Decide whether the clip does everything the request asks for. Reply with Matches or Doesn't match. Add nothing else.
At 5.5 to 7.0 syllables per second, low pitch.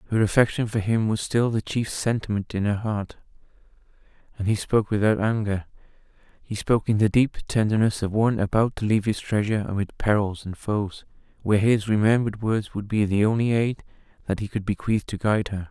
Matches